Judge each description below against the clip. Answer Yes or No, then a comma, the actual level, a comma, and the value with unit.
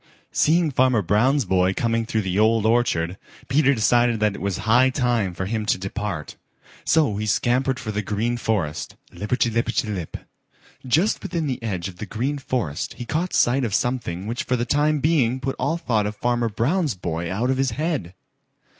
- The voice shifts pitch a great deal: No, average, 4.2 semitones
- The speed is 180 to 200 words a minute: Yes, average, 190 wpm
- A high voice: No, low, 115 Hz